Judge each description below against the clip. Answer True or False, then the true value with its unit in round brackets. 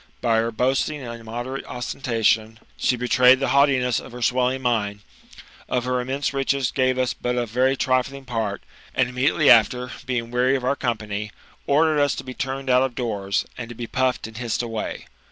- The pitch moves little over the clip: True (2.1 semitones)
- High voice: False (125 Hz)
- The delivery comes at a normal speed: True (190 wpm)